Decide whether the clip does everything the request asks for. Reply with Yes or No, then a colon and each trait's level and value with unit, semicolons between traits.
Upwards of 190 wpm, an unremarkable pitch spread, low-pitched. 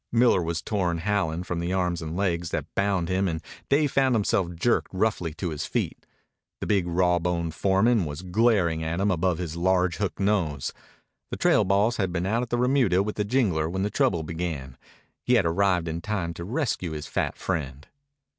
Yes: average, 200 wpm; average, 3.5 semitones; very low, 90 Hz